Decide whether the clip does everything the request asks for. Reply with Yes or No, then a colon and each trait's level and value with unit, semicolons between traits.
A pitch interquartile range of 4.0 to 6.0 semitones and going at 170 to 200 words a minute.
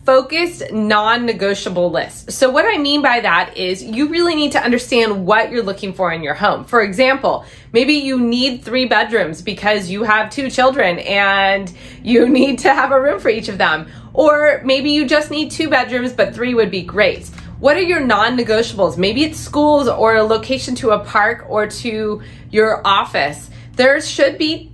Yes: average, 4.7 semitones; average, 190 wpm